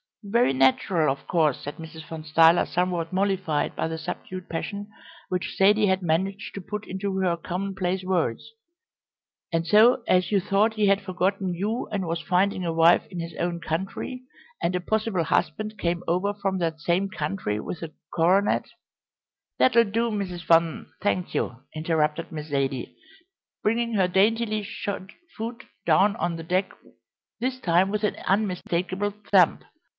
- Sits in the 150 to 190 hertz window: Yes, medium, 185 Hz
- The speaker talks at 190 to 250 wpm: No, average, 160 wpm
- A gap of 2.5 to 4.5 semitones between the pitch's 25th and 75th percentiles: Yes, average, 3.3 semitones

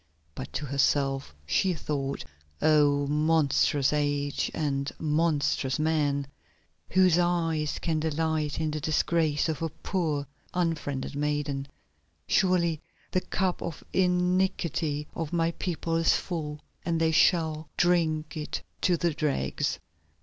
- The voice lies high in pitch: No, medium, 155 Hz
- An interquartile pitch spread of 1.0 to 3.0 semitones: Yes, narrow, 2.5 semitones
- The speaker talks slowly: Yes, slow, 120 wpm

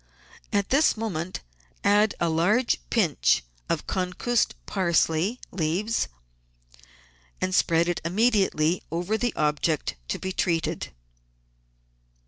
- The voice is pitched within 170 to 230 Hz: Yes, medium, 185 Hz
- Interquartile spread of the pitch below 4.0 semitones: No, average, 4.5 semitones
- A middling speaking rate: No, slow, 105 wpm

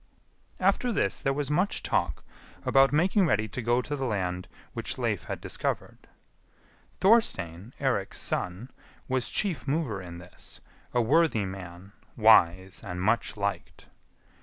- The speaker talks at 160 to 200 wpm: No, slow, 135 wpm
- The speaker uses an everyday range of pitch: No, wide, 7.3 semitones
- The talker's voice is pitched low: Yes, low, 115 Hz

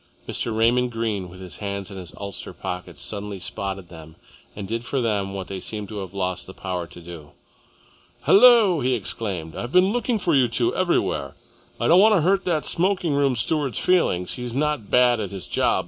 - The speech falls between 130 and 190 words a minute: No, average, 200 wpm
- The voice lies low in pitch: Yes, low, 110 Hz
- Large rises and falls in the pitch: Yes, wide, 7.8 semitones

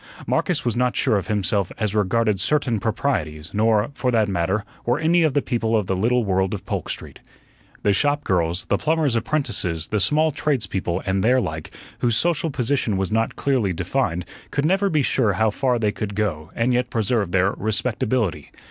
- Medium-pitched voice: No, low, 110 Hz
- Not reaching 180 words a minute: No, average, 190 wpm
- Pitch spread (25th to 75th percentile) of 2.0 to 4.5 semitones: No, average, 5.1 semitones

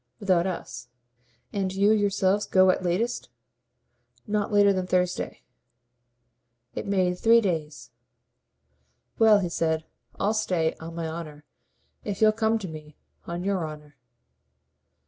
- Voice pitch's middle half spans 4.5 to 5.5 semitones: No, average, 4.0 semitones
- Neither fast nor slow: No, slow, 130 wpm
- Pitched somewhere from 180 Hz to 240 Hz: Yes, medium, 185 Hz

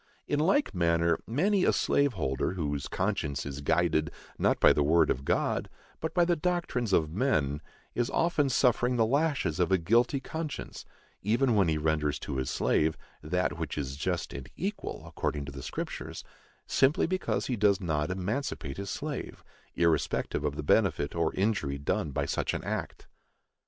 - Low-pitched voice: Yes, very low, 90 Hz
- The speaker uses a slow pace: No, average, 170 wpm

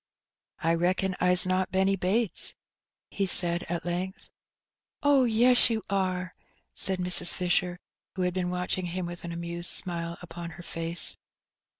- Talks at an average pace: Yes, average, 150 wpm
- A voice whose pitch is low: No, medium, 180 Hz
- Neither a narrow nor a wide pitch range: No, narrow, 1.5 semitones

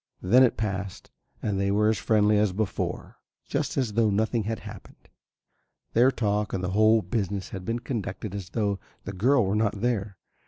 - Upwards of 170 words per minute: Yes, average, 185 wpm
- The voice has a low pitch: Yes, low, 105 Hz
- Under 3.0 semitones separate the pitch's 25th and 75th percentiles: Yes, narrow, 2.4 semitones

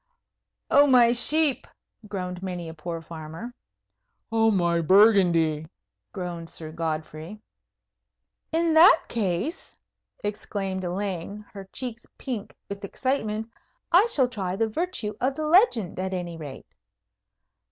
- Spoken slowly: Yes, slow, 120 wpm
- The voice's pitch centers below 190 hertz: No, high, 200 Hz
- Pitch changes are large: Yes, wide, 5.9 semitones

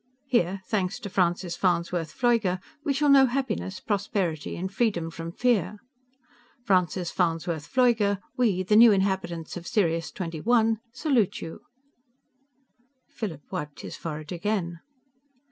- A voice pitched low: No, high, 190 Hz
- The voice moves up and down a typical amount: Yes, average, 4.8 semitones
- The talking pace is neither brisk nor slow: No, slow, 125 wpm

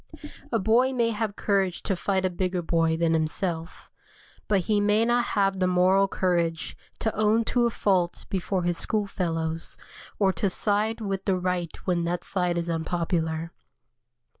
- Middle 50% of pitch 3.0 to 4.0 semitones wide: Yes, average, 3.3 semitones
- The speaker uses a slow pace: No, average, 165 wpm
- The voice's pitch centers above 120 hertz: Yes, medium, 185 Hz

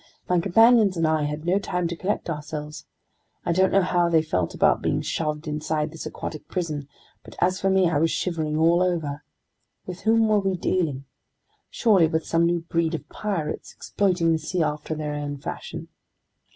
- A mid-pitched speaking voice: Yes, medium, 165 Hz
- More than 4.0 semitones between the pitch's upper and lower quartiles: No, average, 3.2 semitones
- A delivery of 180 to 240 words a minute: Yes, average, 185 wpm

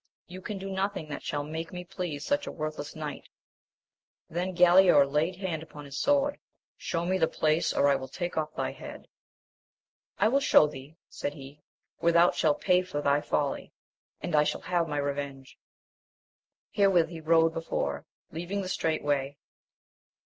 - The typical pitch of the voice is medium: Yes, medium, 160 Hz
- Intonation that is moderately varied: Yes, average, 3.7 semitones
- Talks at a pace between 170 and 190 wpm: Yes, average, 180 wpm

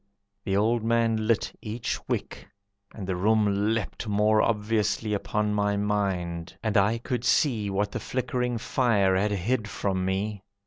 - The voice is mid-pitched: No, low, 105 Hz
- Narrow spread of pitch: Yes, narrow, 2.1 semitones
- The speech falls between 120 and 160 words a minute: Yes, average, 150 wpm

